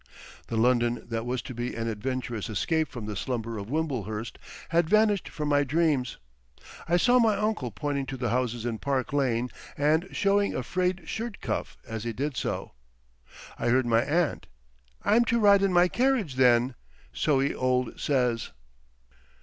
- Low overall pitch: Yes, low, 130 Hz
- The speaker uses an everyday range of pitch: No, wide, 6.5 semitones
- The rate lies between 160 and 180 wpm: Yes, average, 170 wpm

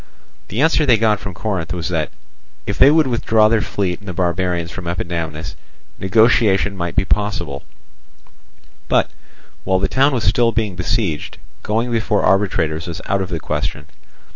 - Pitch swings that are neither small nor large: Yes, average, 4.3 semitones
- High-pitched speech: No, very low, 95 Hz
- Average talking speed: Yes, average, 165 wpm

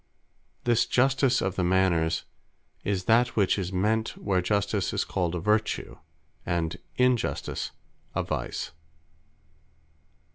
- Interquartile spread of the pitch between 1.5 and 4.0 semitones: Yes, average, 3.7 semitones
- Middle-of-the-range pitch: No, low, 100 Hz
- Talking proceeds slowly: Yes, slow, 115 wpm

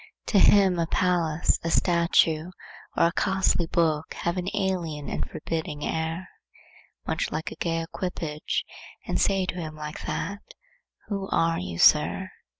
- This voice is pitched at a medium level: Yes, medium, 170 Hz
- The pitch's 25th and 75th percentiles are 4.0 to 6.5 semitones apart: No, average, 2.7 semitones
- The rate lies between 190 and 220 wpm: No, average, 150 wpm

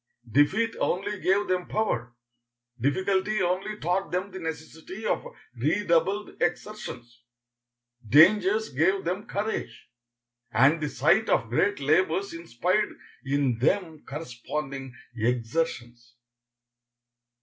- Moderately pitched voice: Yes, medium, 165 Hz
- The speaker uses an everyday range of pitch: No, wide, 6.5 semitones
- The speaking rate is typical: No, slow, 100 wpm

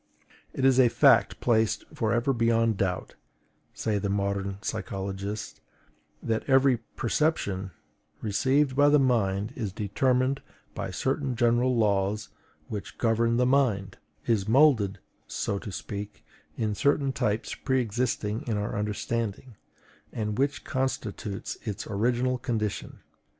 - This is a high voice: No, low, 115 Hz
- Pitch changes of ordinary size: Yes, average, 3.9 semitones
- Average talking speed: No, slow, 125 wpm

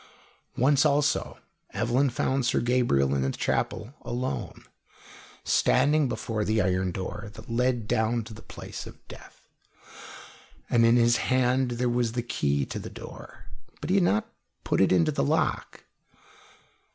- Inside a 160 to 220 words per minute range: No, average, 150 wpm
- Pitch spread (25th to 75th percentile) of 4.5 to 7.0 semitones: No, average, 3.1 semitones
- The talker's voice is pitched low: Yes, low, 120 Hz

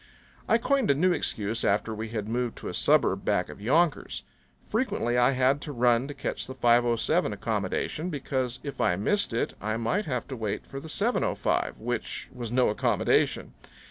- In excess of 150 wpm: Yes, average, 180 wpm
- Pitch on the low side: Yes, low, 125 Hz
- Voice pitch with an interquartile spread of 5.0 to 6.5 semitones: No, average, 4.0 semitones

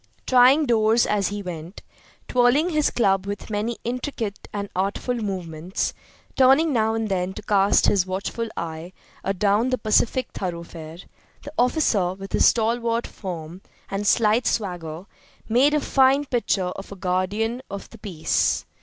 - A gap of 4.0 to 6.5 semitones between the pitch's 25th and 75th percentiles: Yes, average, 4.5 semitones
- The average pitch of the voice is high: Yes, high, 210 Hz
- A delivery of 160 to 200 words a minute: No, average, 145 wpm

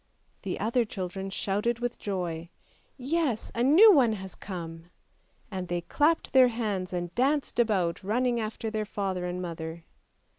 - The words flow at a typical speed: Yes, average, 160 wpm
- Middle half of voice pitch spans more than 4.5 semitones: Yes, average, 5.1 semitones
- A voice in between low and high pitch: No, high, 205 Hz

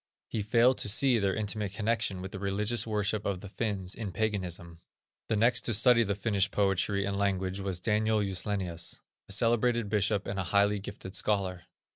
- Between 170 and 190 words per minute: Yes, average, 180 wpm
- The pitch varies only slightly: Yes, narrow, 2.2 semitones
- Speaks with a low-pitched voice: Yes, low, 100 Hz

